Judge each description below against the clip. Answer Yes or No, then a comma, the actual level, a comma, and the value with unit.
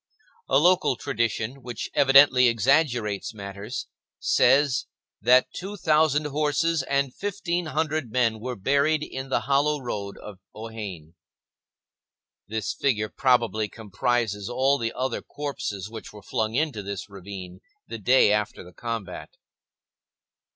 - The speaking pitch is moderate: No, low, 120 Hz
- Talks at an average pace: No, slow, 125 wpm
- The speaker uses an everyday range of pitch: Yes, average, 5.0 semitones